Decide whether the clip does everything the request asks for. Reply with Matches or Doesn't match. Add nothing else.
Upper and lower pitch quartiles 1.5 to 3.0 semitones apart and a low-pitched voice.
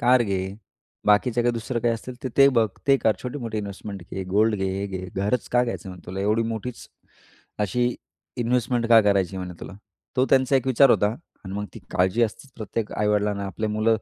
Doesn't match